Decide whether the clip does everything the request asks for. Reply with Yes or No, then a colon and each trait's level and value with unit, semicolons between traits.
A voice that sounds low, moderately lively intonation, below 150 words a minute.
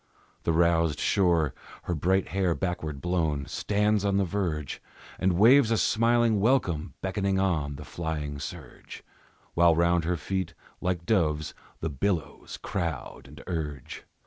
Yes: very low, 85 Hz; average, 3.9 semitones; average, 140 wpm